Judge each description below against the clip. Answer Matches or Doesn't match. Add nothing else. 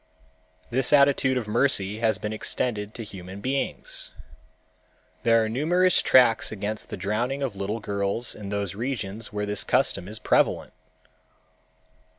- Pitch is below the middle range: Matches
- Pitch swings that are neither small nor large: Matches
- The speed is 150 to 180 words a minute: Doesn't match